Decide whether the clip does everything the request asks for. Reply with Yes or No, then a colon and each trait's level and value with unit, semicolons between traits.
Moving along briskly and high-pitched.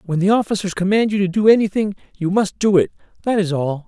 Yes: fast, 230 wpm; high, 195 Hz